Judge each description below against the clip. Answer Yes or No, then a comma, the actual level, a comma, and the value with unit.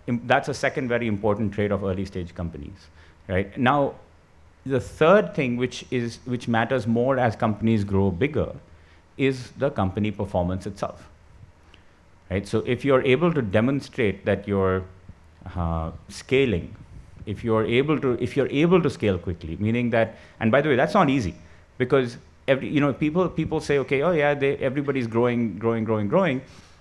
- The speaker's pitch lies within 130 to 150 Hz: No, low, 110 Hz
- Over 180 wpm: No, average, 170 wpm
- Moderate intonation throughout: No, wide, 6.0 semitones